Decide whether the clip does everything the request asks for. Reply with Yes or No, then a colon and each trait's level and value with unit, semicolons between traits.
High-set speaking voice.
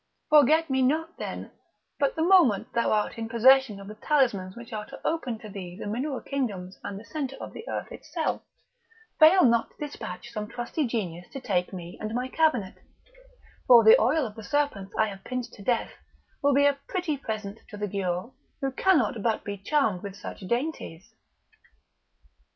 Yes: high, 235 Hz